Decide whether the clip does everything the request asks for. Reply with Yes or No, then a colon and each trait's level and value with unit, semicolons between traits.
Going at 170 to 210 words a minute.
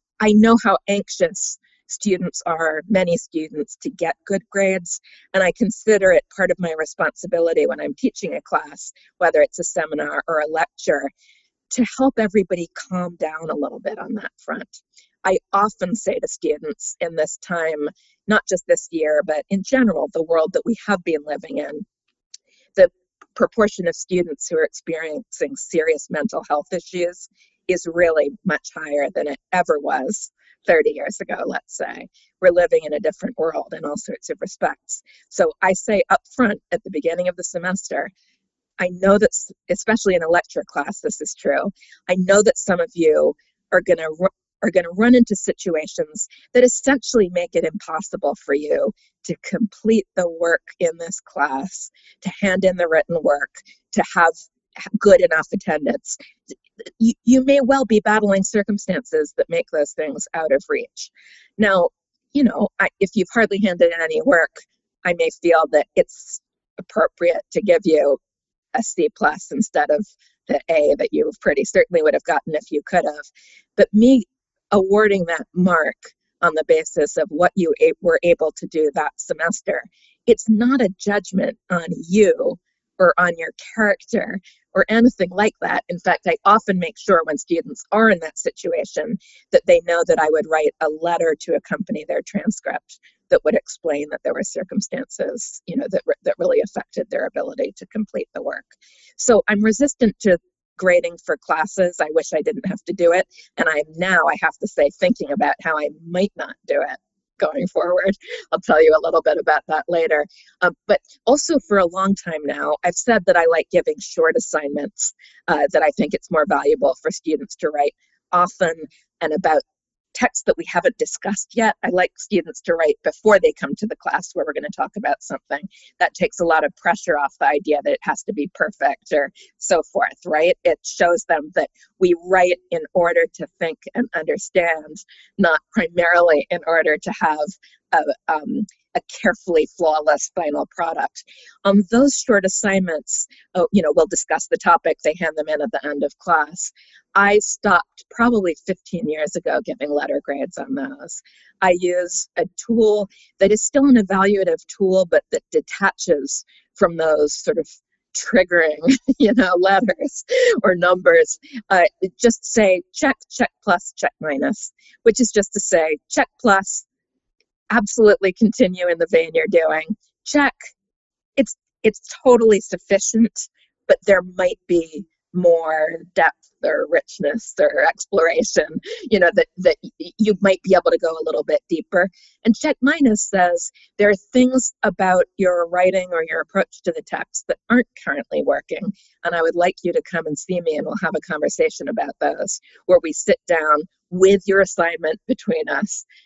Yes: average, 180 wpm